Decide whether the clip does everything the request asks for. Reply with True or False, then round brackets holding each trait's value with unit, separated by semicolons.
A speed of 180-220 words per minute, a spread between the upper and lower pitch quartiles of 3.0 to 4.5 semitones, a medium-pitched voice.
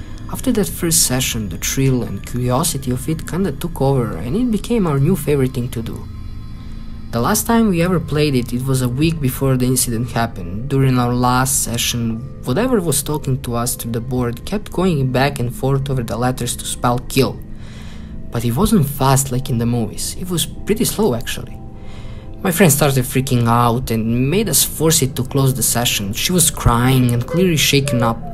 False (200 wpm; 3.7 semitones; 125 Hz)